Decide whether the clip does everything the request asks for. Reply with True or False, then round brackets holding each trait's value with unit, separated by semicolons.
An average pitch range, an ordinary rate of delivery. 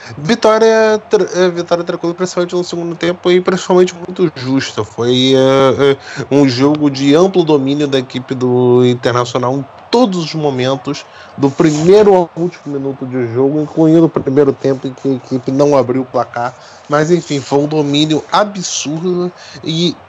True (4.7 semitones; 160 wpm)